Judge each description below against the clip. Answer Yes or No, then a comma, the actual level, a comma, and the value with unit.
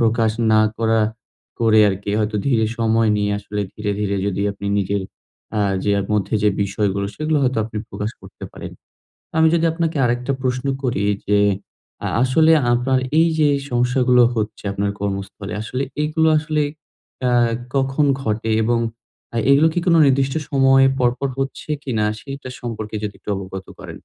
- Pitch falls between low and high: No, low, 115 Hz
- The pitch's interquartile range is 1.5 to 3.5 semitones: No, average, 4.4 semitones